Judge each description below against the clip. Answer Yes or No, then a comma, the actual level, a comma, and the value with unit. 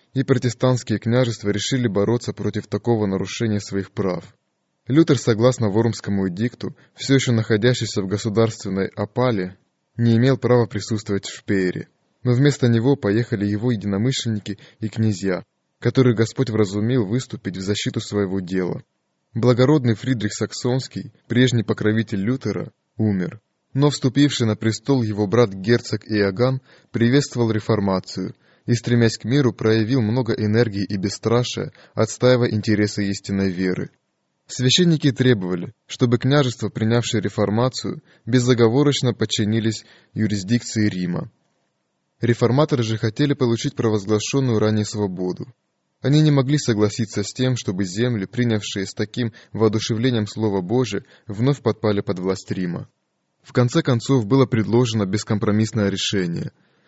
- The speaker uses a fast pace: No, average, 120 wpm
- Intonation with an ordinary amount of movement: Yes, average, 3.4 semitones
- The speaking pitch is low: Yes, low, 115 Hz